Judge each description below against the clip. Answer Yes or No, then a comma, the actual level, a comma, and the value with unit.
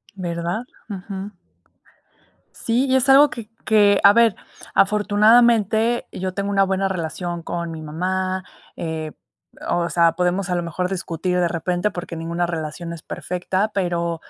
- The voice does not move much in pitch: No, average, 3.1 semitones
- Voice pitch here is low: No, medium, 185 Hz